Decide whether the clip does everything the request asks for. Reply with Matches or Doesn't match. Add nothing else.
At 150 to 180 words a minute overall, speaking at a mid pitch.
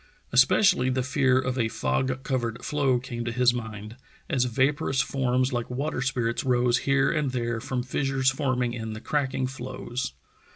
Doesn't match